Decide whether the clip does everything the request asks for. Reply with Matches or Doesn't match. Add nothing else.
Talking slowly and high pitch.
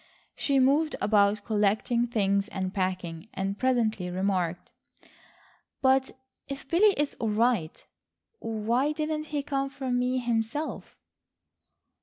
Matches